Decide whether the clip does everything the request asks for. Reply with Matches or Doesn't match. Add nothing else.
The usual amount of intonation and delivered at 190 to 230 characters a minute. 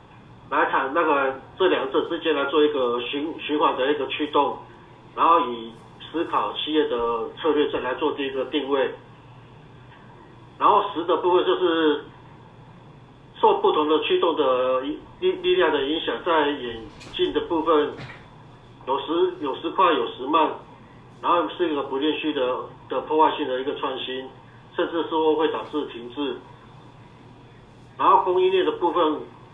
Matches